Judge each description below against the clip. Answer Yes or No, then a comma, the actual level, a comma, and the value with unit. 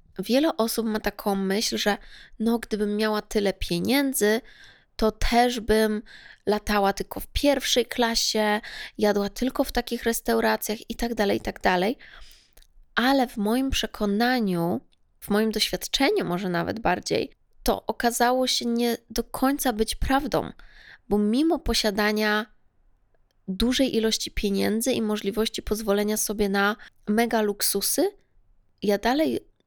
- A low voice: No, high, 220 Hz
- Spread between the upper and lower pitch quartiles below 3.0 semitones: Yes, narrow, 2.5 semitones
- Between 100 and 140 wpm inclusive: Yes, average, 125 wpm